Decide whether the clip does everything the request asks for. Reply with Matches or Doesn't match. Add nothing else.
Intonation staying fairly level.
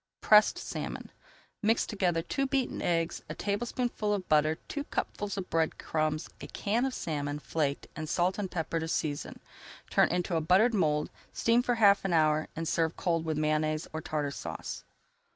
Doesn't match